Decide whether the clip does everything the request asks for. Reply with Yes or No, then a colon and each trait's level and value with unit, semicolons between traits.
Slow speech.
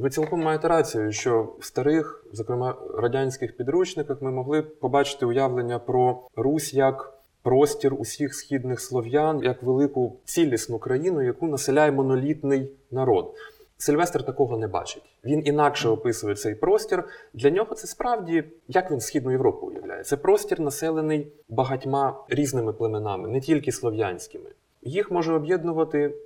No: average, 135 wpm